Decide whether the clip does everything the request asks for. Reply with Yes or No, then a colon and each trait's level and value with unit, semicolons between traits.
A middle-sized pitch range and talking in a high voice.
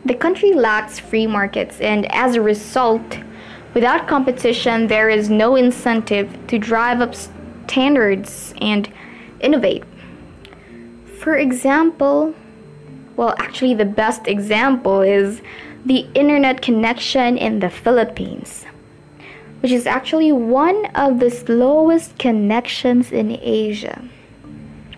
Yes: average, 3.6 semitones; high, 235 Hz